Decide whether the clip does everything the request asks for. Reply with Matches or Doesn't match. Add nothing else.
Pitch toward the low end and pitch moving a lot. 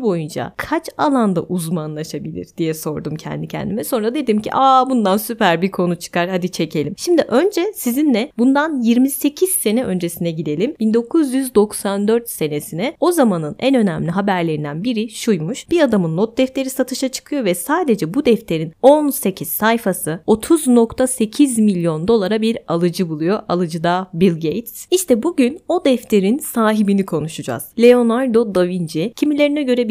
Doesn't match